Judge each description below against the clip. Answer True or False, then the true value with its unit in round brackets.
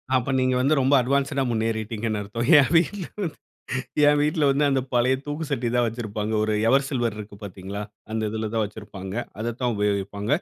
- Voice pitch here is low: True (115 Hz)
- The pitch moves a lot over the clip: False (4.2 semitones)